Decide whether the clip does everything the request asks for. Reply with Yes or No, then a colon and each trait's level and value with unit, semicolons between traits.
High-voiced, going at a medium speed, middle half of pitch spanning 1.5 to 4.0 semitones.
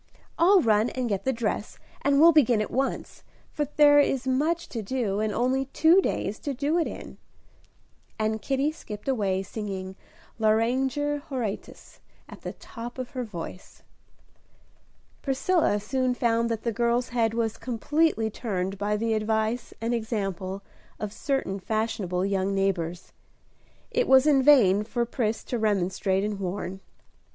No: high, 230 Hz; average, 150 wpm; average, 4.4 semitones